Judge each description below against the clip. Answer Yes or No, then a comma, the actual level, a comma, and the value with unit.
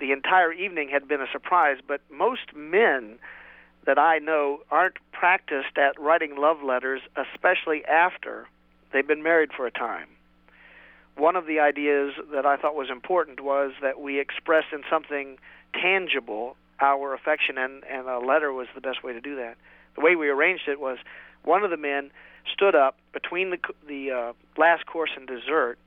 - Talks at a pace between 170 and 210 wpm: Yes, average, 175 wpm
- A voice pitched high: No, medium, 140 Hz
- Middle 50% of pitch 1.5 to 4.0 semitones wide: Yes, average, 2.9 semitones